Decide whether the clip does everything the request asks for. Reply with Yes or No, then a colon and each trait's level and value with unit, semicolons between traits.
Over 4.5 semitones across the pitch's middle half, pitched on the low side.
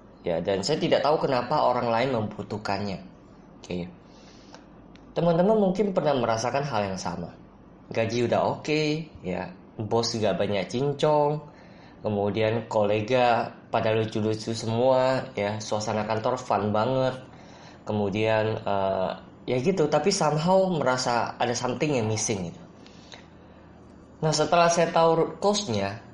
Yes: wide, 5.6 semitones; low, 115 Hz